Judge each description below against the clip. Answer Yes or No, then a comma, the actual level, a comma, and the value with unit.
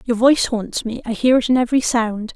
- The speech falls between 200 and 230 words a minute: No, fast, 255 wpm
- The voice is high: Yes, high, 240 Hz